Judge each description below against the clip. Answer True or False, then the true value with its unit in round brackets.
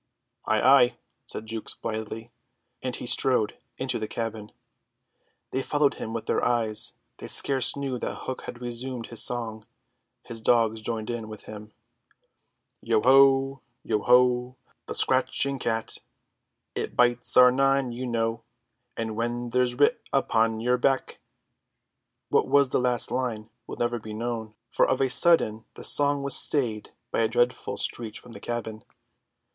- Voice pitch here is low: True (120 Hz)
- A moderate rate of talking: True (155 wpm)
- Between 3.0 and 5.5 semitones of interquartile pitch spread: False (2.5 semitones)